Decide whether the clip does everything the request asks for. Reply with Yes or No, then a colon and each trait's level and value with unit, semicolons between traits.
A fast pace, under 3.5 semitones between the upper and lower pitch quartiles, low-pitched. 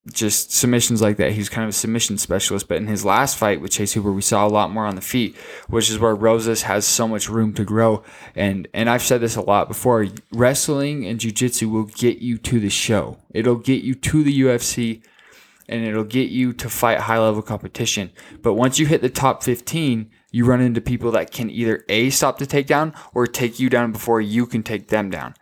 Yes: fast, 225 wpm; narrow, 2.5 semitones; low, 115 Hz